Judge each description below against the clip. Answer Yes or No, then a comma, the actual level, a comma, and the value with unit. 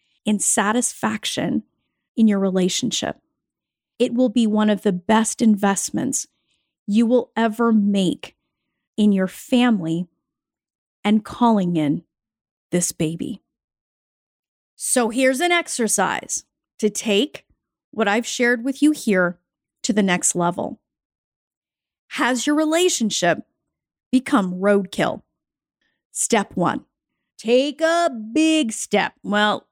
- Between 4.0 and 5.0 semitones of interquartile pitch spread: Yes, average, 4.5 semitones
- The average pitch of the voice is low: No, high, 220 Hz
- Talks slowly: Yes, slow, 105 wpm